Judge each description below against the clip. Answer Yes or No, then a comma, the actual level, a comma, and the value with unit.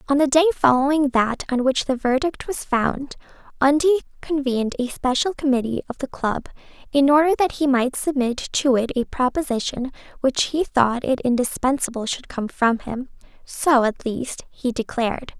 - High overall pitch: Yes, very high, 265 Hz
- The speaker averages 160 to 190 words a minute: Yes, average, 170 wpm